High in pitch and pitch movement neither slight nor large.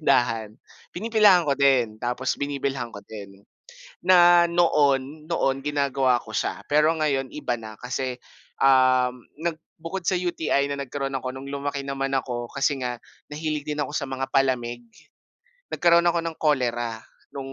No: medium, 140 Hz; average, 3.5 semitones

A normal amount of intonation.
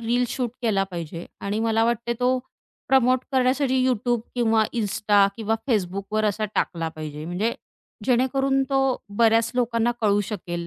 Yes: average, 3.8 semitones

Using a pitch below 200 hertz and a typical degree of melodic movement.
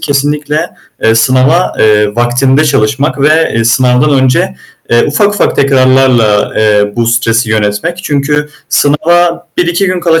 Yes: low, 135 Hz; average, 4.9 semitones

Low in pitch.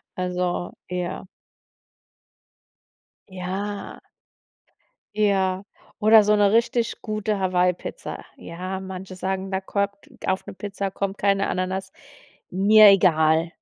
No: high, 190 Hz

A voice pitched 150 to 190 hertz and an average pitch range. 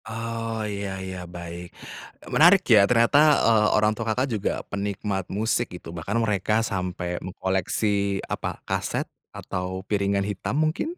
No: low, 100 Hz; average, 3.3 semitones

